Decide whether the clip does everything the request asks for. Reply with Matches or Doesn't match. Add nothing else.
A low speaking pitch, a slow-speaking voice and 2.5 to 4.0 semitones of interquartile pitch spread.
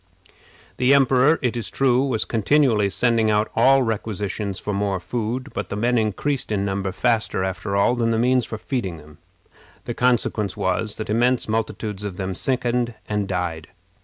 Doesn't match